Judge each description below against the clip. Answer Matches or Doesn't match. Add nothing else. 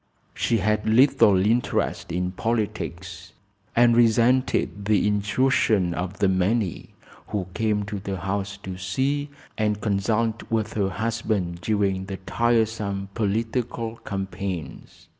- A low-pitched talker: Matches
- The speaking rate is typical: Doesn't match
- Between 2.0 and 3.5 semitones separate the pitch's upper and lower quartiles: Matches